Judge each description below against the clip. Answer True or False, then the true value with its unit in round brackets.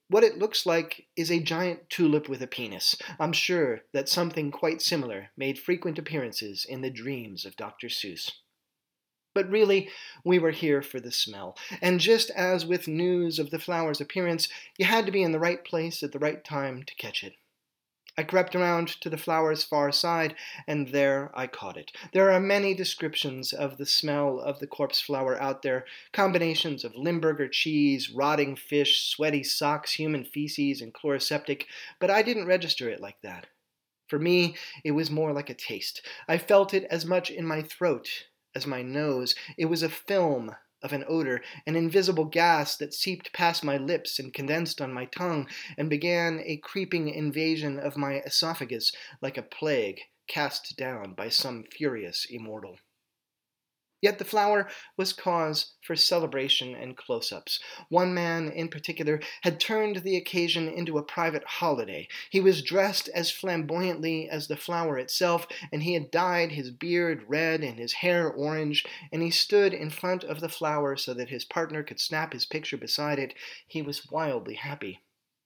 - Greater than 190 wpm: False (175 wpm)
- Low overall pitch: False (160 Hz)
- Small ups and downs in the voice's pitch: False (3.4 semitones)